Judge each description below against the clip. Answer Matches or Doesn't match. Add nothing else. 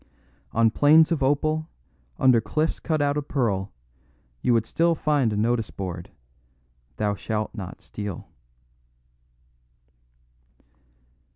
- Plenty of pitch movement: Matches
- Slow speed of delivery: Matches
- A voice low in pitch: Matches